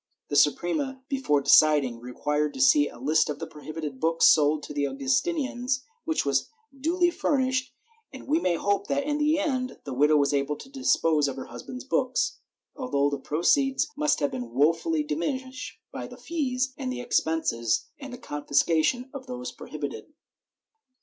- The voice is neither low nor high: Yes, medium, 165 Hz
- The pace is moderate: Yes, average, 165 wpm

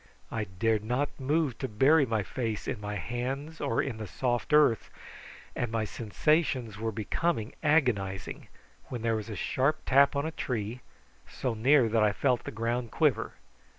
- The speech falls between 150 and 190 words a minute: Yes, average, 170 wpm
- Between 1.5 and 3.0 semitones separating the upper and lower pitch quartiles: No, average, 4.2 semitones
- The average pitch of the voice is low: Yes, low, 120 Hz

